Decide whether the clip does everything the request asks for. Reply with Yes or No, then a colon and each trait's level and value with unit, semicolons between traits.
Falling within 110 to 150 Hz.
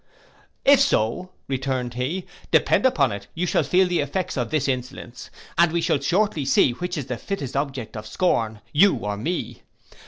Yes: medium, 140 Hz